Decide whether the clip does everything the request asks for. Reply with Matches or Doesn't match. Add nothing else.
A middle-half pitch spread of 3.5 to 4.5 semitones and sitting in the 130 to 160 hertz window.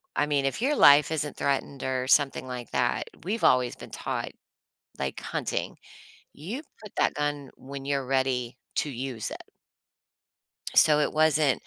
Doesn't match